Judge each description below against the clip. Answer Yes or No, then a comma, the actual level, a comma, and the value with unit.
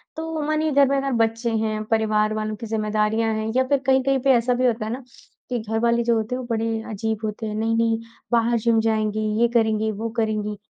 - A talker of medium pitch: No, high, 225 Hz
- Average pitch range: No, narrow, 2.0 semitones